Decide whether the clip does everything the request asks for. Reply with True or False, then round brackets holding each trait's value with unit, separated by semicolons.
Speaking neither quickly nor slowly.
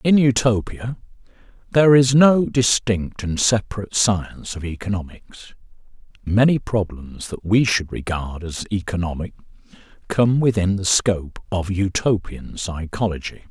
False (115 wpm)